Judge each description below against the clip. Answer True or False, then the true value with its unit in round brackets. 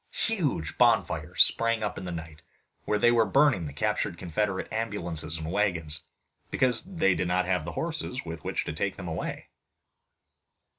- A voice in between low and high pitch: False (95 Hz)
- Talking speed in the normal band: True (165 wpm)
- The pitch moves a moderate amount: False (5.8 semitones)